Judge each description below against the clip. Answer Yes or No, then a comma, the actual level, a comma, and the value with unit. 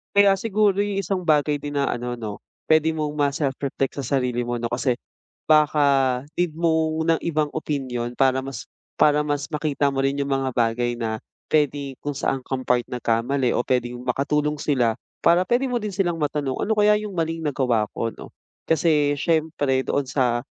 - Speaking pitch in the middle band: Yes, medium, 145 Hz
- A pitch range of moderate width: Yes, average, 3.8 semitones